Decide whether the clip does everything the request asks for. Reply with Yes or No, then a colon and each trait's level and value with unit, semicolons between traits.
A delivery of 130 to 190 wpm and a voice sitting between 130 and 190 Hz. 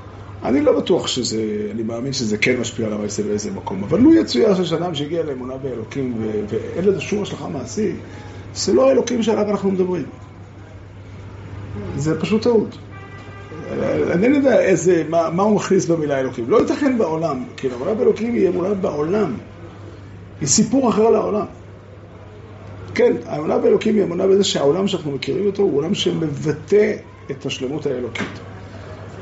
Yes: fast, 150 wpm; low, 135 Hz